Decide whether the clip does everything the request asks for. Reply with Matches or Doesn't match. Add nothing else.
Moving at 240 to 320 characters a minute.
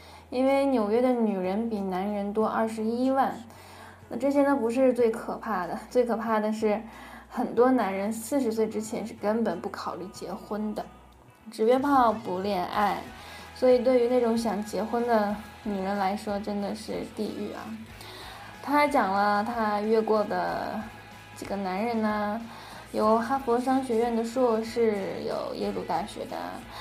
Doesn't match